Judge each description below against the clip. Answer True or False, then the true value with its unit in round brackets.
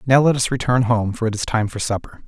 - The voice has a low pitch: True (120 Hz)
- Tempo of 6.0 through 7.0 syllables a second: True (6.1 syllables/s)